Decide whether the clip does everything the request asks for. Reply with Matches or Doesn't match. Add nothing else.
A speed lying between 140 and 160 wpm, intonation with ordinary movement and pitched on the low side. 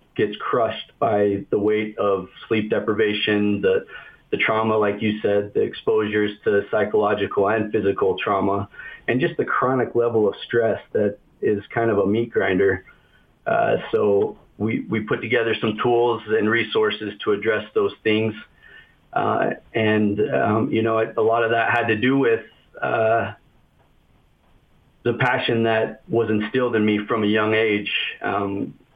Doesn't match